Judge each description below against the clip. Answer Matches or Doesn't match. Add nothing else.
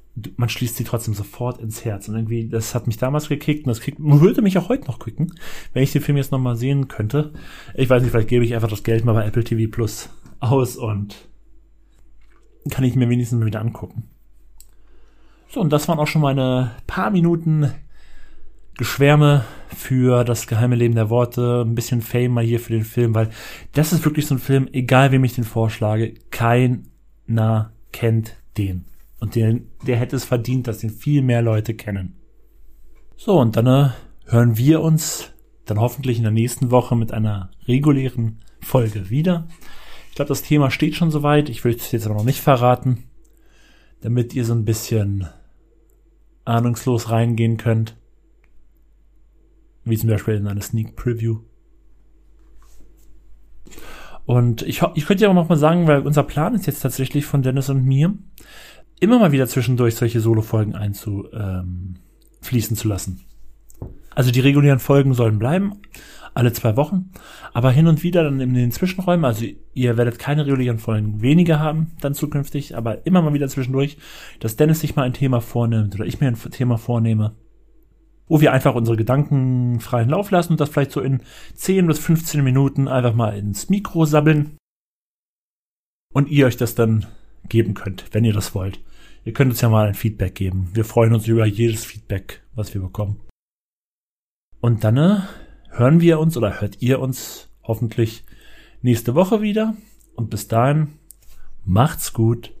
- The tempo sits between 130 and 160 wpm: Doesn't match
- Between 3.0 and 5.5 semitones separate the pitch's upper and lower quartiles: Matches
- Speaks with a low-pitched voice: Matches